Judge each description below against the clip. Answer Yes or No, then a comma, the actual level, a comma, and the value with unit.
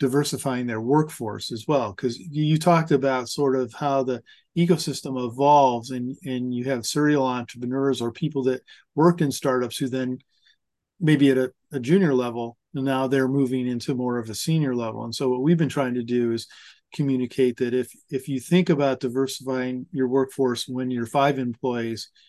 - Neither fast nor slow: Yes, average, 180 wpm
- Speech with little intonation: Yes, narrow, 2.2 semitones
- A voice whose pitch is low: Yes, low, 130 Hz